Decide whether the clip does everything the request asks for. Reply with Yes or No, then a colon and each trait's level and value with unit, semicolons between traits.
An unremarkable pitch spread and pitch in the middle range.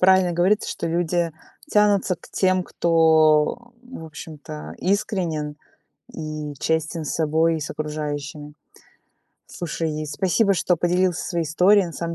Yes: average, 3.1 semitones; medium, 165 Hz